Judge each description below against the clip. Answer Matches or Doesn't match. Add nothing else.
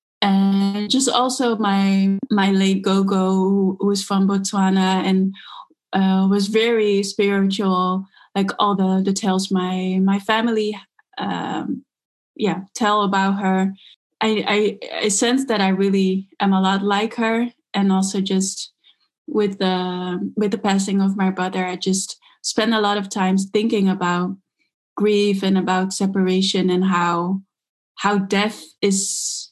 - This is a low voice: Doesn't match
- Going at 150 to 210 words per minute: Doesn't match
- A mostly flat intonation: Matches